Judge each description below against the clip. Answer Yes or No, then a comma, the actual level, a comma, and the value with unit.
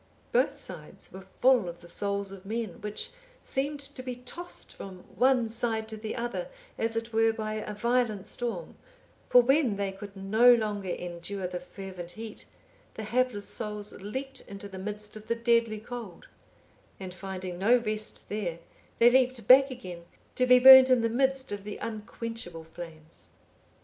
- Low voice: No, high, 215 Hz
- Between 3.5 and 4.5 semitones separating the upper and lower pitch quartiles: Yes, average, 3.9 semitones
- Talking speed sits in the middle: Yes, average, 170 wpm